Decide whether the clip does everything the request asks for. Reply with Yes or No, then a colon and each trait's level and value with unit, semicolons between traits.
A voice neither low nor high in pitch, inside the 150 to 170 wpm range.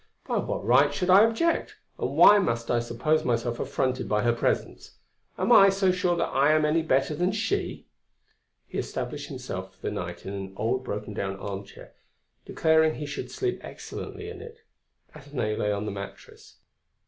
No: medium, 145 Hz; average, 180 wpm